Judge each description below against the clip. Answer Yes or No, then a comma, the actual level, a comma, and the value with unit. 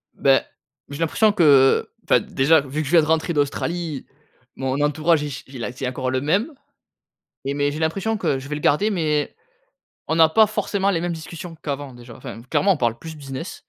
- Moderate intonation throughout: Yes, average, 3.7 semitones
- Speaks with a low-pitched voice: No, medium, 150 Hz